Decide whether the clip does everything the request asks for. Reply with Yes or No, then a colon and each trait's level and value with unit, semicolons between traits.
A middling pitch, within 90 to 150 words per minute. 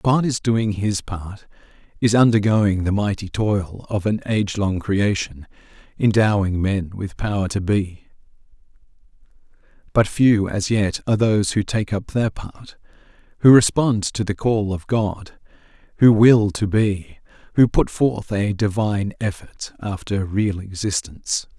No: low, 105 Hz; average, 145 wpm